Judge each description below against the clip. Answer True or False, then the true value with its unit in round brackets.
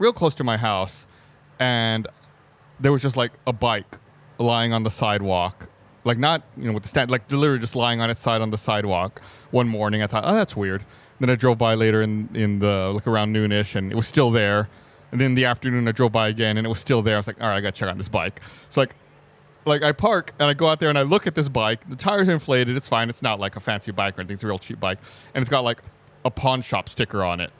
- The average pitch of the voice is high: False (115 Hz)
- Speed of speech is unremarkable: False (275 wpm)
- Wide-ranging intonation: False (4.3 semitones)